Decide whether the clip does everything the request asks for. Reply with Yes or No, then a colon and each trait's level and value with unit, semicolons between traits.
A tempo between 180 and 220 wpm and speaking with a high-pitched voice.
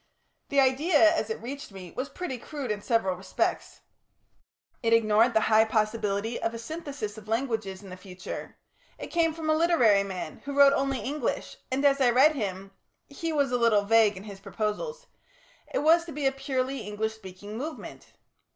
Yes: average, 185 wpm; high, 230 Hz